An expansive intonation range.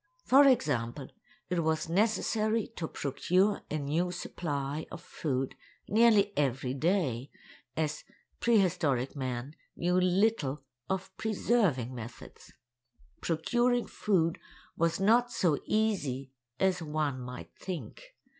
Yes: wide, 6.7 semitones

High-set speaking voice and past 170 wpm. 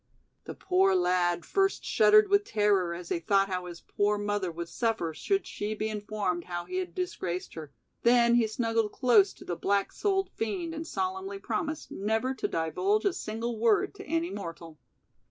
Yes: high, 220 Hz; average, 180 wpm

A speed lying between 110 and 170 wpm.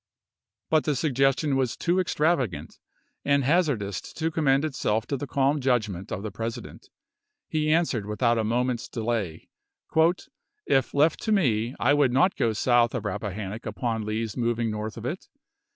Yes: average, 160 wpm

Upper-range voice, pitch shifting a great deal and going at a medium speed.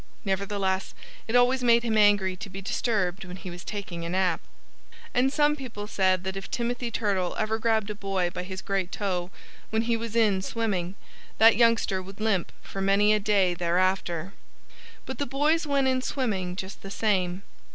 No: high, 200 Hz; average, 3.5 semitones; average, 185 wpm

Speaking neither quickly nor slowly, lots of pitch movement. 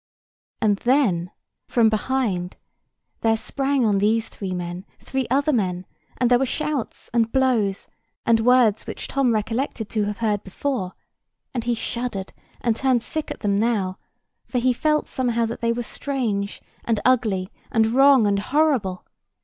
No: average, 155 wpm; average, 4.0 semitones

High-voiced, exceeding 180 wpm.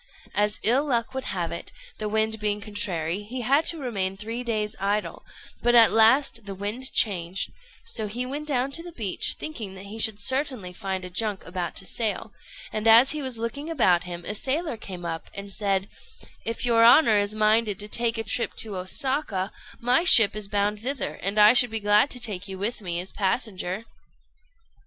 Yes: high, 215 Hz; average, 200 wpm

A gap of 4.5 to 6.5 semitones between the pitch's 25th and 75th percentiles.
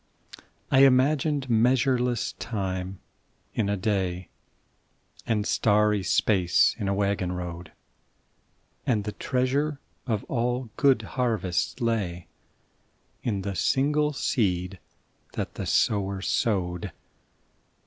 Yes: average, 4.9 semitones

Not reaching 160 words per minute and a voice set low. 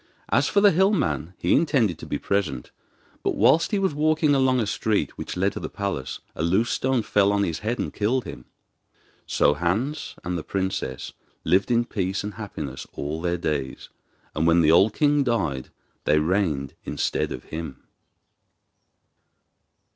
No: average, 170 wpm; low, 100 Hz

